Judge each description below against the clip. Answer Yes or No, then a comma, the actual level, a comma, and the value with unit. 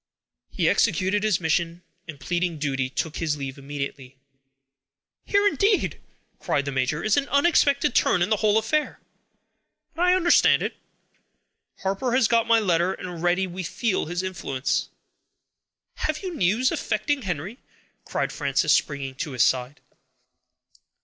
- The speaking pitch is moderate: Yes, medium, 180 Hz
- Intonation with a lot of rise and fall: Yes, wide, 7.9 semitones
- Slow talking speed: No, average, 145 wpm